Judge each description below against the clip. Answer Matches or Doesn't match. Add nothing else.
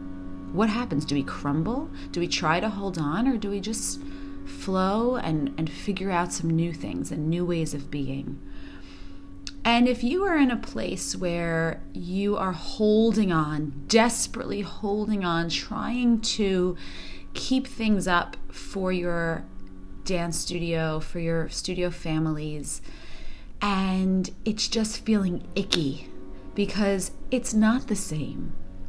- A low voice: Doesn't match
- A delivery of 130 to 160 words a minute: Matches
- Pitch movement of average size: Doesn't match